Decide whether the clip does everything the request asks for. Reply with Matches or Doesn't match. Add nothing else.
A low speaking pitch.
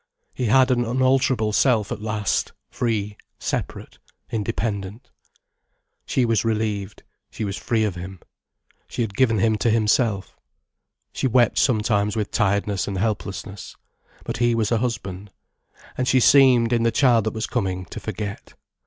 Matches